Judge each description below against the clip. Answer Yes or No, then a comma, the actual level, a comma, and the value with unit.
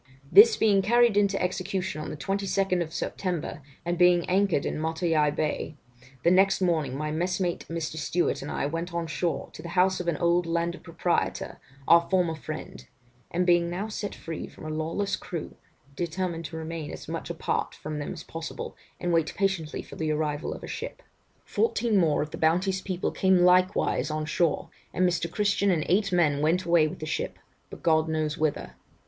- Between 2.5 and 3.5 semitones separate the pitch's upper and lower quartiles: Yes, average, 2.9 semitones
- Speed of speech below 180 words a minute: No, average, 190 wpm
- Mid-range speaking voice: Yes, medium, 170 Hz